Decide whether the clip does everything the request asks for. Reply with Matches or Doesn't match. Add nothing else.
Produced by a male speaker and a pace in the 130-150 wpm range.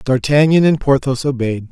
Matches